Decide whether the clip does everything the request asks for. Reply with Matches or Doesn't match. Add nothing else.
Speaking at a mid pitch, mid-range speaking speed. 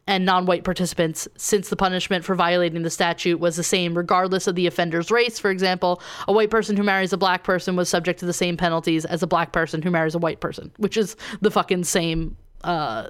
Doesn't match